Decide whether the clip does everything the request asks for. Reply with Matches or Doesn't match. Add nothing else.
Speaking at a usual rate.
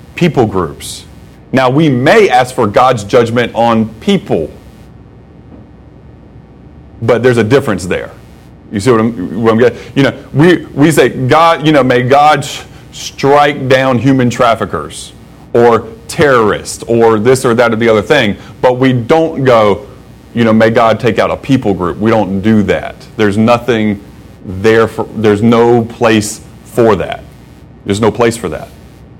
Matches